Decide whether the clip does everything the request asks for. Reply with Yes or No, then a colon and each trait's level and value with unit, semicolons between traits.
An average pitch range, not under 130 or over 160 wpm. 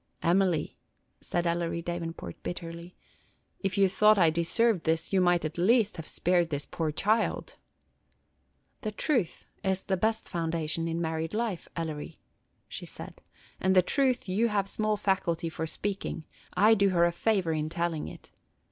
Yes: average, 3.4 semitones; average, 155 wpm